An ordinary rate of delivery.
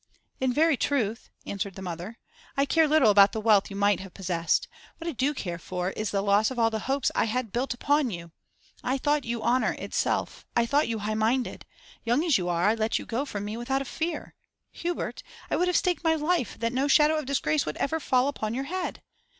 No: fast, 230 wpm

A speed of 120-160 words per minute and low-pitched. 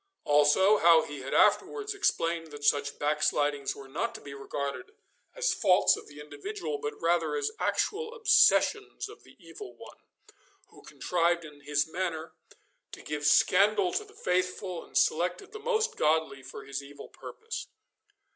No: average, 155 wpm; medium, 165 Hz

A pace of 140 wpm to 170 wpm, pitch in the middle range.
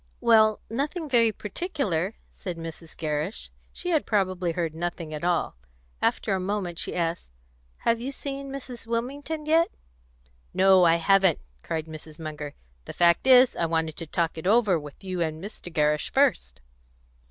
Yes: average, 160 wpm; medium, 180 Hz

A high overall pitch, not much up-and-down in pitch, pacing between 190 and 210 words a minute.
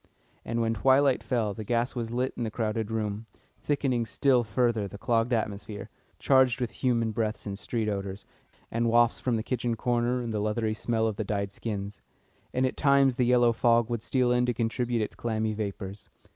No: low, 115 Hz; narrow, 2.3 semitones; average, 195 wpm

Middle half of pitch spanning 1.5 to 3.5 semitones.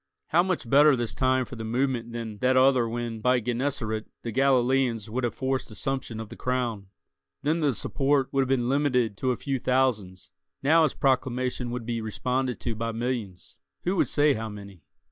Yes: average, 2.8 semitones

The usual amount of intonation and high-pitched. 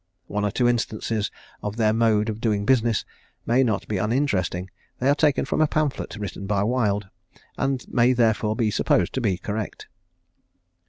No: average, 3.0 semitones; low, 110 Hz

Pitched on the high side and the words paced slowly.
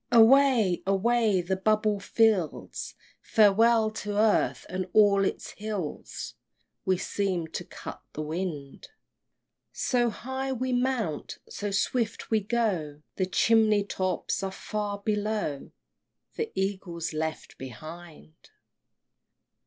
Yes: high, 205 Hz; slow, 115 wpm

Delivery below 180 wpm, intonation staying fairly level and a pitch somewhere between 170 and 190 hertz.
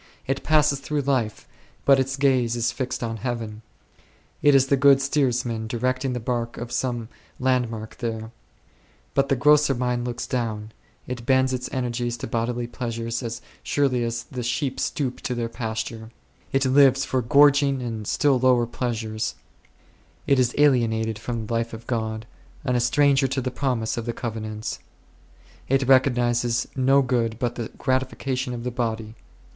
No: average, 165 wpm; narrow, 2.3 semitones; low, 125 Hz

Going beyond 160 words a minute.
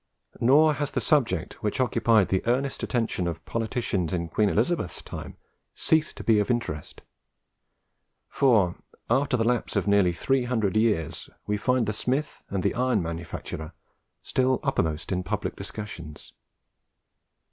No: average, 145 wpm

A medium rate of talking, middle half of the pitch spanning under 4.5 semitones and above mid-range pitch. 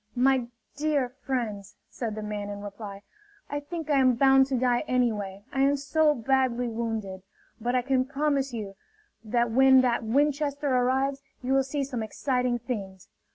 Yes: average, 165 wpm; average, 3.4 semitones; very high, 255 Hz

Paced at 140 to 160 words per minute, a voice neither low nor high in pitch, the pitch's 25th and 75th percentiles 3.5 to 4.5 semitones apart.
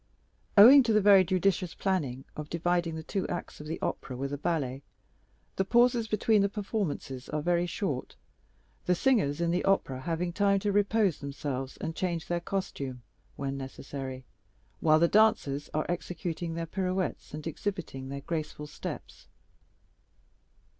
No: average, 155 wpm; medium, 170 Hz; average, 5.3 semitones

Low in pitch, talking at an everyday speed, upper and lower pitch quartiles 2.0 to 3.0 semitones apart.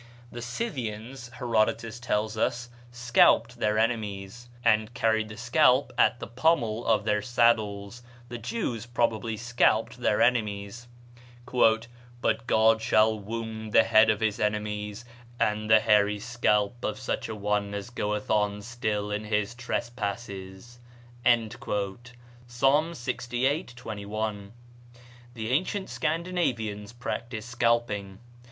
No: low, 115 Hz; slow, 120 wpm; narrow, 2.4 semitones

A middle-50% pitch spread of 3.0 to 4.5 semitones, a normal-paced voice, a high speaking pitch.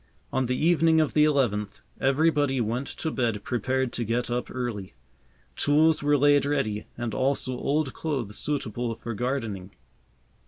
No: average, 3.8 semitones; average, 150 wpm; low, 130 Hz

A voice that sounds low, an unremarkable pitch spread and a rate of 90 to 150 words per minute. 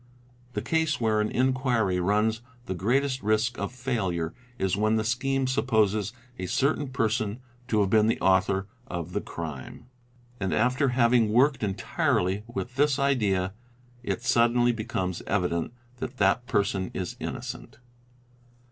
Yes: low, 110 Hz; average, 4.8 semitones; average, 140 wpm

